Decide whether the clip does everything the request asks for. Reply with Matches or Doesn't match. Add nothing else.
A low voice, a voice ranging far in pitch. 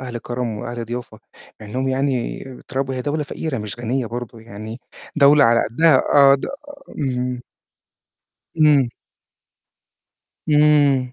Doesn't match